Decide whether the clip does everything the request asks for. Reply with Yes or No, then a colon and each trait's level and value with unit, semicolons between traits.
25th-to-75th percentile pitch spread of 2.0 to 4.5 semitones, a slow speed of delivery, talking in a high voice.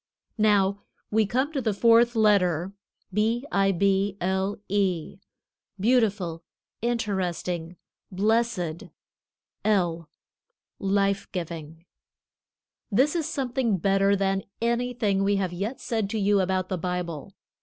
Yes: average, 3.4 semitones; slow, 110 wpm; high, 195 Hz